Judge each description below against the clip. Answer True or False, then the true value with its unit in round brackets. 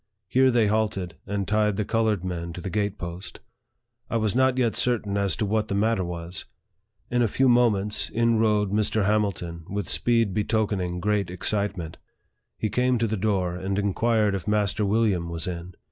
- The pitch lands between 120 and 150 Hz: False (105 Hz)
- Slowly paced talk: False (185 wpm)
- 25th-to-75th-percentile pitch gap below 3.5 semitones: True (2.9 semitones)